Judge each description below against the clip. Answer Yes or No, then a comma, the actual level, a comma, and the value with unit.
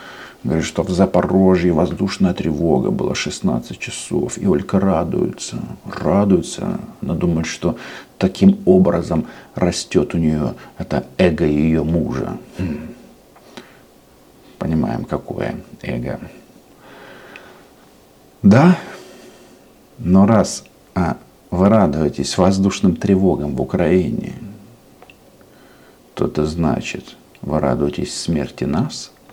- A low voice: Yes, very low, 85 Hz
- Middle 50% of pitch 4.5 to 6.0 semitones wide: No, average, 4.0 semitones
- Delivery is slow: Yes, slow, 90 wpm